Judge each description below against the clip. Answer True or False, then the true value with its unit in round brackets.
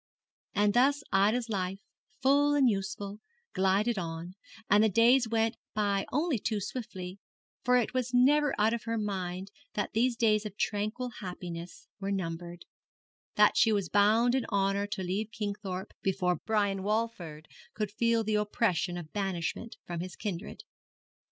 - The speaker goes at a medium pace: True (150 wpm)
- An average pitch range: True (3.3 semitones)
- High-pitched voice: True (205 Hz)